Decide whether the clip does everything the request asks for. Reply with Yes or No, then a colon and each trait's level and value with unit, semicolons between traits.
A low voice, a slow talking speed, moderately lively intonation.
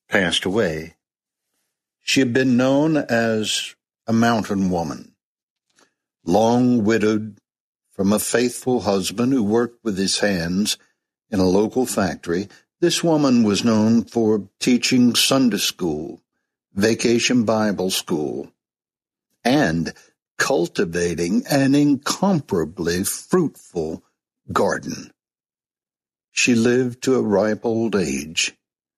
Yes: low, 115 Hz; slow, 100 wpm; average, 3.4 semitones